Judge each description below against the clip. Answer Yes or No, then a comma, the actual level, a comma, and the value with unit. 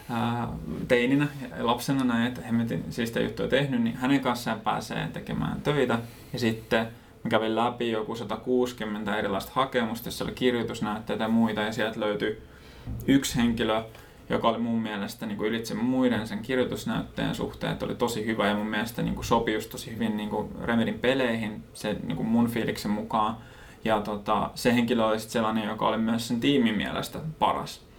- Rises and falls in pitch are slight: Yes, narrow, 2.3 semitones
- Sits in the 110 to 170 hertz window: Yes, low, 115 Hz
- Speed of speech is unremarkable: No, fast, 170 wpm